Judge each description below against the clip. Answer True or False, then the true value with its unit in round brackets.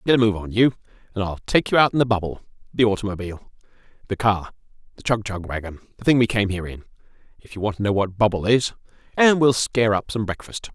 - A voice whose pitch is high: False (105 Hz)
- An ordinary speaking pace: False (220 wpm)